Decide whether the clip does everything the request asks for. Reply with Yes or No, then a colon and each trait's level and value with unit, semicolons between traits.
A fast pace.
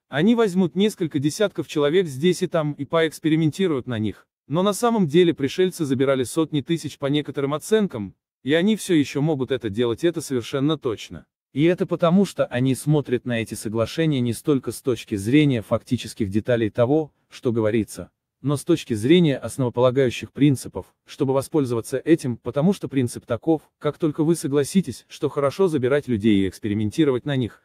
Yes: fast, 165 wpm